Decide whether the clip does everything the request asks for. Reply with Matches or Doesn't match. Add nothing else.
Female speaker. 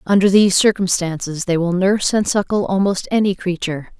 Matches